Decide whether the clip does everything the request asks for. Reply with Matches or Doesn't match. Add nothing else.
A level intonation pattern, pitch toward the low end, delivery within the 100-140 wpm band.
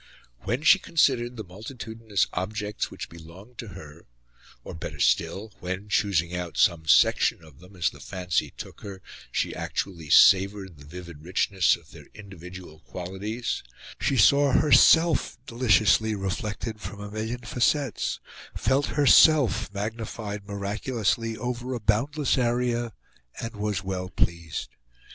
Doesn't match